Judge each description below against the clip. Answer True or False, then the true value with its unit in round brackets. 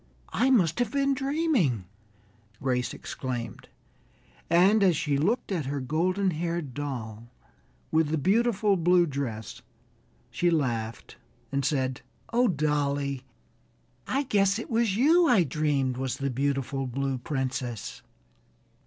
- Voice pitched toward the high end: False (150 Hz)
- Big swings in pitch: True (7.0 semitones)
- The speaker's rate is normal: False (125 wpm)